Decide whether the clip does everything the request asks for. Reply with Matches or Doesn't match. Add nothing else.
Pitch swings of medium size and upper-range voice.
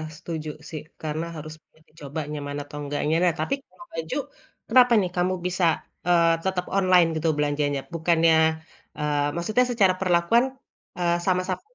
Doesn't match